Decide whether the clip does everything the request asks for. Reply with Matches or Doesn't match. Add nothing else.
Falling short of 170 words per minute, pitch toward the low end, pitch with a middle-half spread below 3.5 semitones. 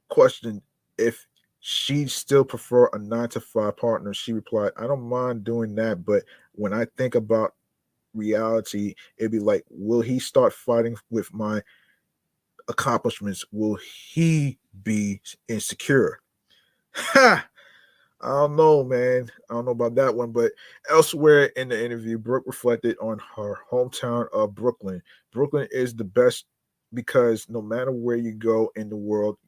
Matches